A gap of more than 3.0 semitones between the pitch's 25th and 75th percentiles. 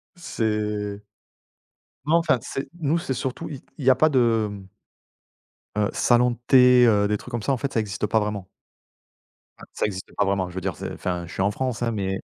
Yes: average, 4.1 semitones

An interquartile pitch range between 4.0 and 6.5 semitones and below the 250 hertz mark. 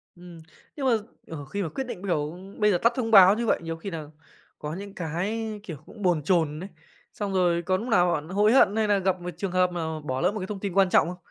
No: average, 3.6 semitones; medium, 185 Hz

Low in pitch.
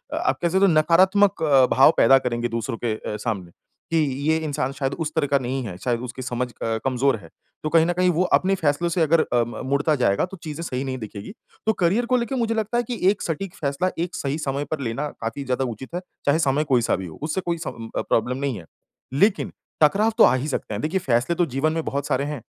No: medium, 145 Hz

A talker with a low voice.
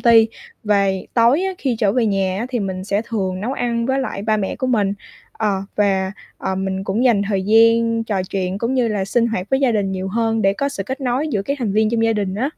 No: high, 215 Hz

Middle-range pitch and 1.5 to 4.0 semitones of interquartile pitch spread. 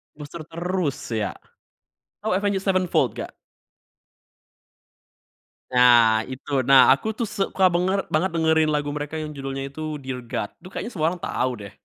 No: medium, 155 Hz; average, 5.2 semitones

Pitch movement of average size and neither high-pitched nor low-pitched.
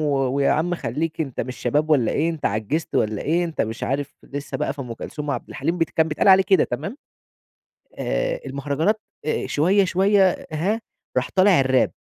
Yes: average, 4.7 semitones; medium, 155 Hz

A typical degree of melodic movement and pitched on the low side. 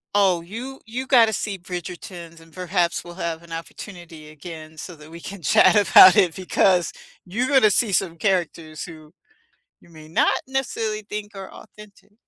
No: average, 3.9 semitones; medium, 180 Hz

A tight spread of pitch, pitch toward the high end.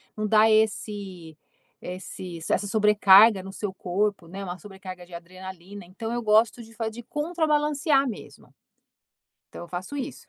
No: average, 3.5 semitones; high, 205 Hz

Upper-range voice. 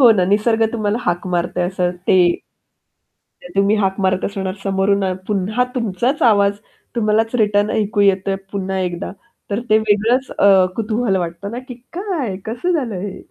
Yes: high, 205 Hz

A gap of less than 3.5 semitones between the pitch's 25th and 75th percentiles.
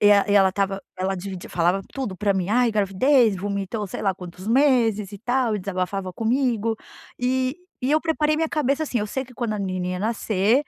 No: average, 4.6 semitones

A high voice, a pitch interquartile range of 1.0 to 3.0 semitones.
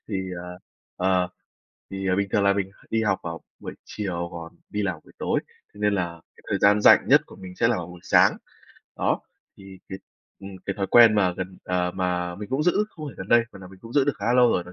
No: very low, 95 Hz; narrow, 2.6 semitones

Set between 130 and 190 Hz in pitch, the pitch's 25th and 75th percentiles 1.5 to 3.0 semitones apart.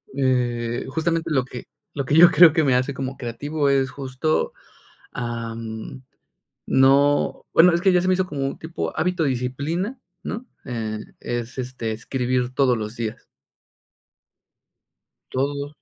No: low, 135 Hz; average, 4.3 semitones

